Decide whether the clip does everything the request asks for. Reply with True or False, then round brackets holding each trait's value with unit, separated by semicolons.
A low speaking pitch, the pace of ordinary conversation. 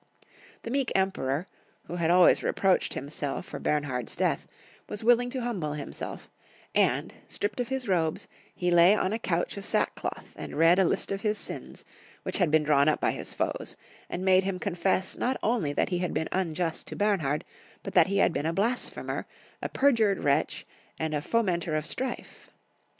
False (180 Hz; 185 wpm)